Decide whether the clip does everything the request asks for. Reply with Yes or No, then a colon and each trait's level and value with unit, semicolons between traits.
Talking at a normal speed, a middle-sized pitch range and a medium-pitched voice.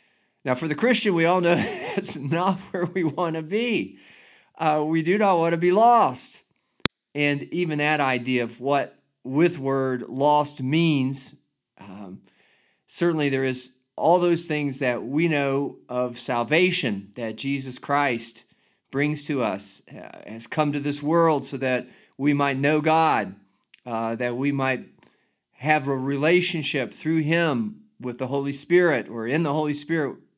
Yes: average, 155 wpm; average, 4.2 semitones; medium, 145 Hz